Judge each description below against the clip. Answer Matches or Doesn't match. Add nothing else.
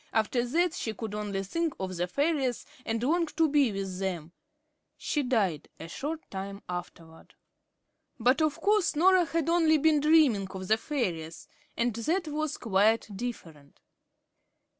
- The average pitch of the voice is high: Matches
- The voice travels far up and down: Matches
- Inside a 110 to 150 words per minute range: Matches